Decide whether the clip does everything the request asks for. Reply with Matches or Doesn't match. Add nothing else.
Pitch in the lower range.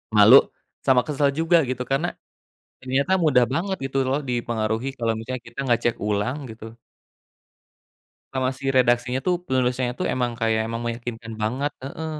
Matches